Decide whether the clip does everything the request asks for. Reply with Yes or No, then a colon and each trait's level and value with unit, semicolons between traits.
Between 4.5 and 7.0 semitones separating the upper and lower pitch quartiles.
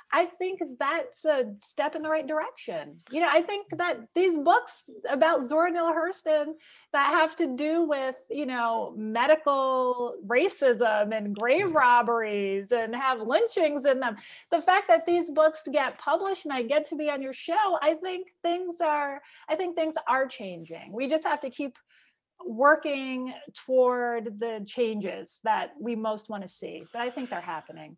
Yes: average, 5.3 semitones